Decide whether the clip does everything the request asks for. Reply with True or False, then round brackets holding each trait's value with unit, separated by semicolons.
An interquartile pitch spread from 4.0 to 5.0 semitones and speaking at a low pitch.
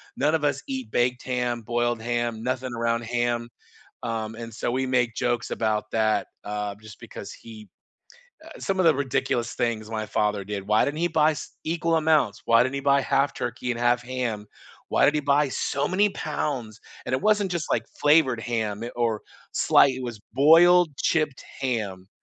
True (4.4 semitones; 120 Hz)